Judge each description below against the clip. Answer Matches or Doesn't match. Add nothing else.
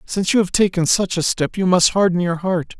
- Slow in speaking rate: Doesn't match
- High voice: Doesn't match